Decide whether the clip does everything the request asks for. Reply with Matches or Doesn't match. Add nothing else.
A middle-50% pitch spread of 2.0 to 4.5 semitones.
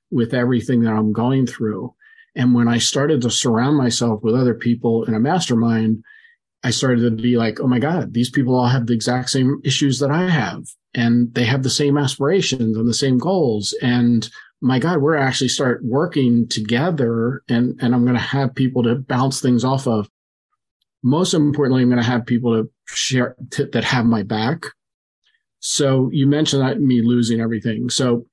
Matches